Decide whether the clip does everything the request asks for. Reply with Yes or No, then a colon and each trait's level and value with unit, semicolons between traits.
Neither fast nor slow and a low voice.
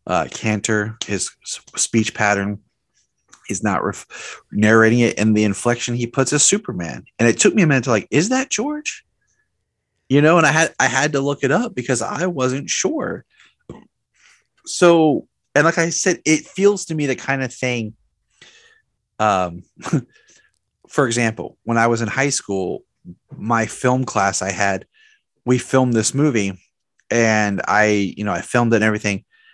Yes: average, 170 wpm; low, 125 Hz